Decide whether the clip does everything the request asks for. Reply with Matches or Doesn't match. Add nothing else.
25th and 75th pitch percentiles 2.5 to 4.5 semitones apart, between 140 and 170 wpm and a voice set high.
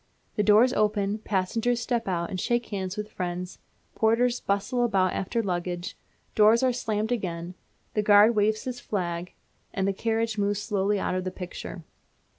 Matches